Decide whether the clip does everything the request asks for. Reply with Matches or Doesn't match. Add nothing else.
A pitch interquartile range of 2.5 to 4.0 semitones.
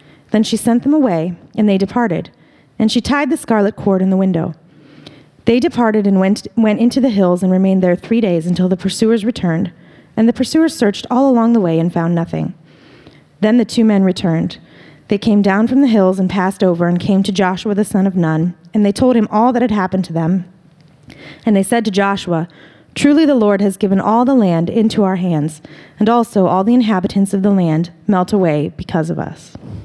Doesn't match